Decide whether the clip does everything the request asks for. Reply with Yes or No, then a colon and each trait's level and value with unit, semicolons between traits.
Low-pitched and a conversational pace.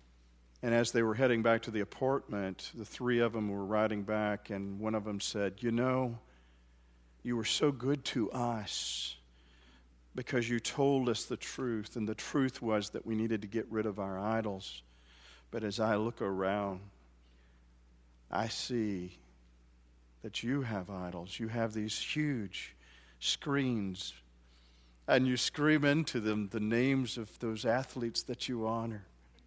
Yes: low, 105 Hz; average, 155 wpm